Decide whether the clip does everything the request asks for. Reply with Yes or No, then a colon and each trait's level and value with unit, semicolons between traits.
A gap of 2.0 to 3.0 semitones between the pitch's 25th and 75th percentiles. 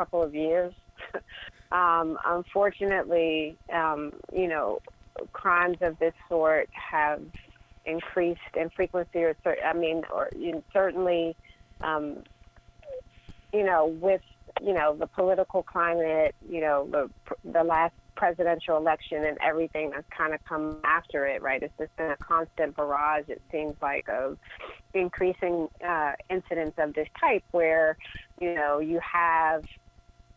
Yes: narrow, 2.4 semitones